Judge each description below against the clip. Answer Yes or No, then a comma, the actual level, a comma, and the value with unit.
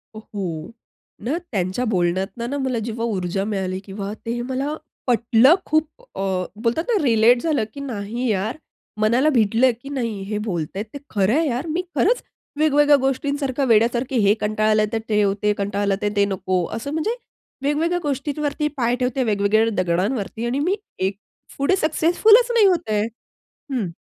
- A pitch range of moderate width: No, wide, 5.7 semitones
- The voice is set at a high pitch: Yes, high, 235 Hz